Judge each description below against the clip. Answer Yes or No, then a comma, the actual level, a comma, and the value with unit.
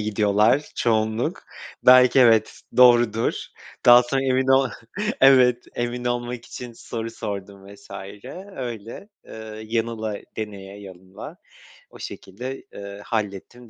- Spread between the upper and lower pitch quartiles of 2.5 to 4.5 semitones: Yes, average, 2.8 semitones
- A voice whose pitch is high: No, low, 115 Hz